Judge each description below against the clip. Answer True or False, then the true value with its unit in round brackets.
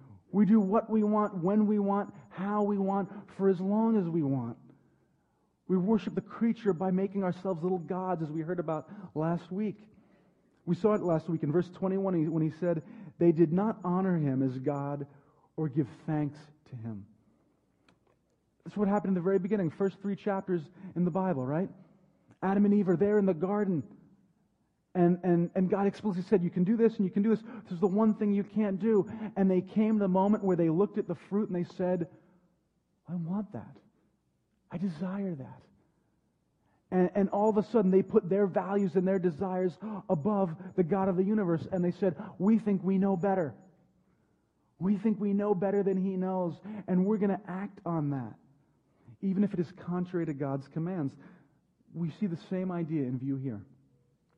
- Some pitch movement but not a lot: True (3.0 semitones)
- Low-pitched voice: False (190 Hz)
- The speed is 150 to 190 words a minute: False (200 wpm)